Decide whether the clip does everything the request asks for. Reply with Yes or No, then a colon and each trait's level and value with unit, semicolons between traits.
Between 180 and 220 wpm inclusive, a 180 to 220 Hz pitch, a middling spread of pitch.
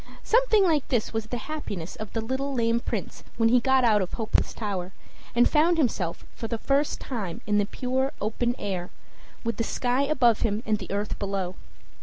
No: average, 195 wpm; high, 230 Hz; average, 4.2 semitones